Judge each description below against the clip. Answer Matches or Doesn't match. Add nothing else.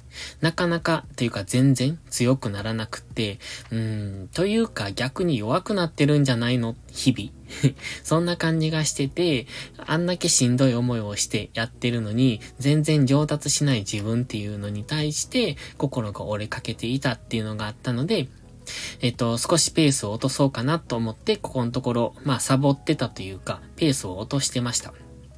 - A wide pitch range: Doesn't match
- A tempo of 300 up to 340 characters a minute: Doesn't match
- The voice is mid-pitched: Doesn't match